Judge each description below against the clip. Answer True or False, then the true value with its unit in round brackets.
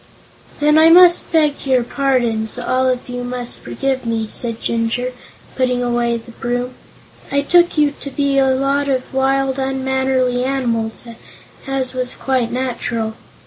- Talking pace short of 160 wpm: True (145 wpm)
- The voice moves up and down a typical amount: False (2.0 semitones)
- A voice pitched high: True (255 Hz)